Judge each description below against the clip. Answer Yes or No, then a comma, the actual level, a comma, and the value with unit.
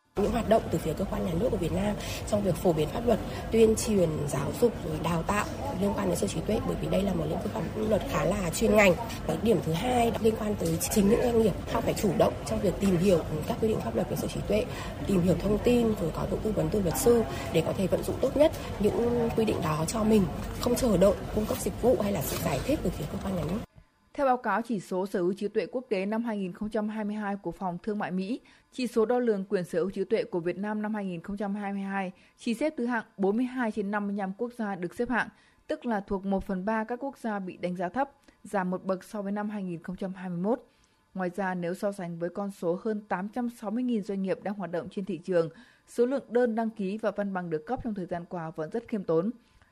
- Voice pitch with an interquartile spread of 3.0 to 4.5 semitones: Yes, average, 3.6 semitones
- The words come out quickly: Yes, fast, 255 wpm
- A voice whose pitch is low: No, high, 205 Hz